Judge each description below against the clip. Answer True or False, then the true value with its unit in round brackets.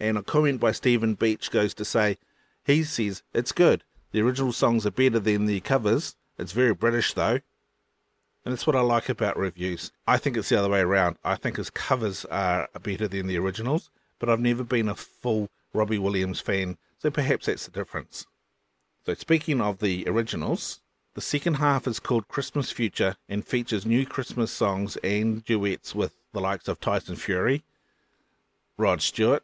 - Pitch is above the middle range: False (110 Hz)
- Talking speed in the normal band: True (180 wpm)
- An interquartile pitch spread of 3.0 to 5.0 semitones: True (3.6 semitones)